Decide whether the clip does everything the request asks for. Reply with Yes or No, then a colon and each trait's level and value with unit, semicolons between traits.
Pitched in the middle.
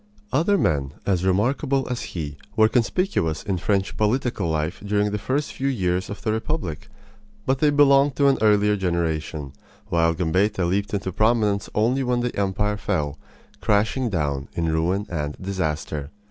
No: low, 100 Hz